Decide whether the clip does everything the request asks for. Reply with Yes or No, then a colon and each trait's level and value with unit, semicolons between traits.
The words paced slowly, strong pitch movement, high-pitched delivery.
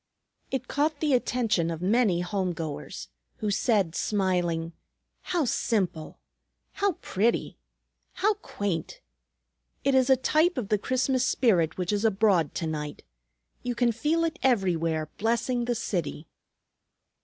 Yes: slow, 130 wpm; wide, 6.9 semitones; high, 215 Hz